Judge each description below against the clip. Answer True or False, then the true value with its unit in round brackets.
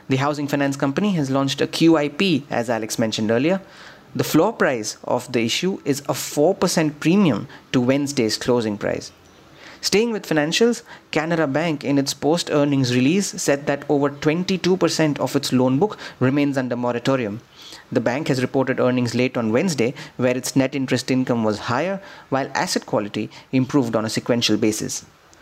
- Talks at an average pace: True (165 wpm)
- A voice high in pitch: False (140 Hz)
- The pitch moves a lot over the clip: False (3.8 semitones)